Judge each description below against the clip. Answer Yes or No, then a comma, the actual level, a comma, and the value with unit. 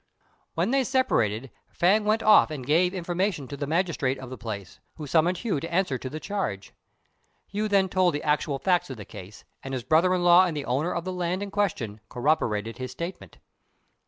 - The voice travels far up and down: Yes, wide, 6.1 semitones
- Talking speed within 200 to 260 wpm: Yes, fast, 205 wpm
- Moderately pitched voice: Yes, medium, 165 Hz